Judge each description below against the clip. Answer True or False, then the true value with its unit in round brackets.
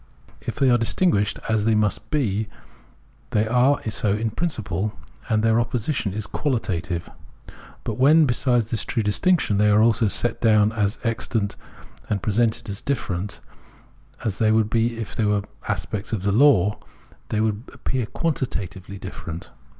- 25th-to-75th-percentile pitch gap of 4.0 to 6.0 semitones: False (2.7 semitones)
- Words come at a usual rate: True (150 wpm)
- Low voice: True (110 Hz)